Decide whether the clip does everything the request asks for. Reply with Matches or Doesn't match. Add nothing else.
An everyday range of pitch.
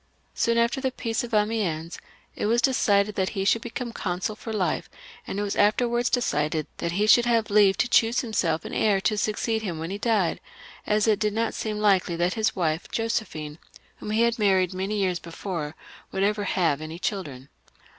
Matches